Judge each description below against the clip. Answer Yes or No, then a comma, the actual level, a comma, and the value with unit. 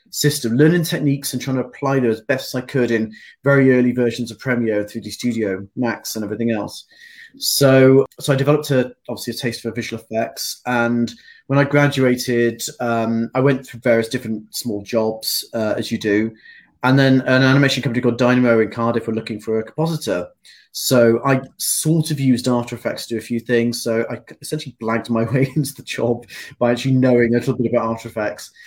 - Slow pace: No, average, 200 wpm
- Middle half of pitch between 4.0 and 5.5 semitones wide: No, average, 2.8 semitones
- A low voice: Yes, low, 120 Hz